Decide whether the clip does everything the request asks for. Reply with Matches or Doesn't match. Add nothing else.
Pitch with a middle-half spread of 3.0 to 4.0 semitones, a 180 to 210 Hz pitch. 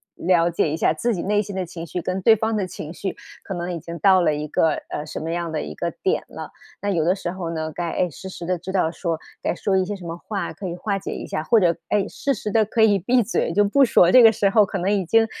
Matches